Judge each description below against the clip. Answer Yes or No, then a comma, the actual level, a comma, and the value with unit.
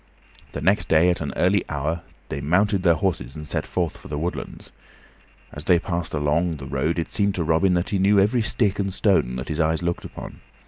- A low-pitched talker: Yes, very low, 85 Hz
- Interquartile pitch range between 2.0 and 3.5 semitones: No, average, 4.1 semitones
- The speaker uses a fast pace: Yes, fast, 220 wpm